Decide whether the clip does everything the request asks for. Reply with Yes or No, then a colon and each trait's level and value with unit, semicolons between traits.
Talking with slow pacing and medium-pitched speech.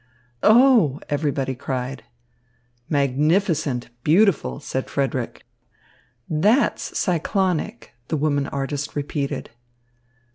Yes: slow, 75 wpm; medium, 145 Hz